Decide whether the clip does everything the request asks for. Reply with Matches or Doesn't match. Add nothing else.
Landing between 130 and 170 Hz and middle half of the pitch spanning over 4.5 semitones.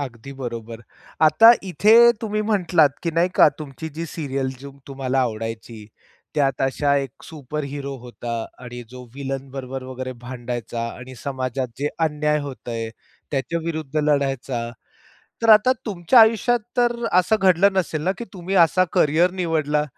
Matches